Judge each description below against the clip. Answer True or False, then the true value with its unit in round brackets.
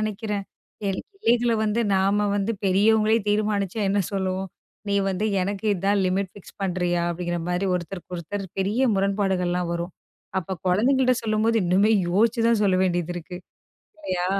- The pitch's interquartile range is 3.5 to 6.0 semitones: False (3.0 semitones)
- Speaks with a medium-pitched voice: False (195 Hz)